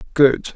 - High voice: No, low, 135 Hz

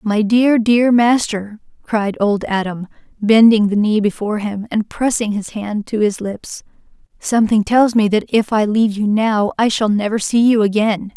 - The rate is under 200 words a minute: Yes, average, 185 wpm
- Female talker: Yes, female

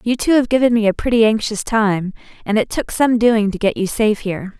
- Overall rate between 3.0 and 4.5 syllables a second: No, 5.8 syllables/s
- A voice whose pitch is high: Yes, high, 220 Hz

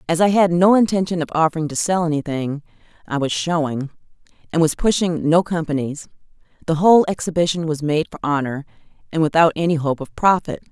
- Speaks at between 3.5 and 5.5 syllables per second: No, 6.0 syllables/s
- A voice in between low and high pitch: Yes, medium, 160 Hz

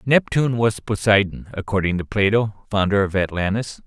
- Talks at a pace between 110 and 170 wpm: Yes, average, 140 wpm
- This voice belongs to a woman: No, male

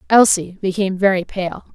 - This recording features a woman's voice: Yes, female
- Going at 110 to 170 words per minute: Yes, average, 140 wpm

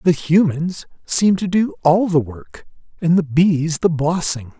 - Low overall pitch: No, medium, 165 Hz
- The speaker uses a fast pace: No, average, 170 wpm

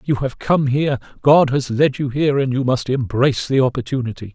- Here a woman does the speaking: No, male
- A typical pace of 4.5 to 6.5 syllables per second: Yes, 5.7 syllables/s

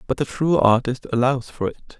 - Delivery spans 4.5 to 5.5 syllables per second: Yes, 5.1 syllables/s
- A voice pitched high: No, low, 130 Hz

